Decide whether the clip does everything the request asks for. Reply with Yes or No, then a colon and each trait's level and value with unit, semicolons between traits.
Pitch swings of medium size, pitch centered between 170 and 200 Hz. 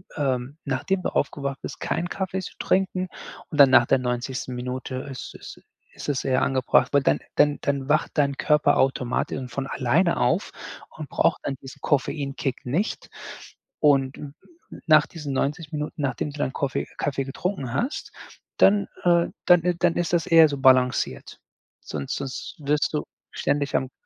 No: average, 3.2 semitones; medium, 140 Hz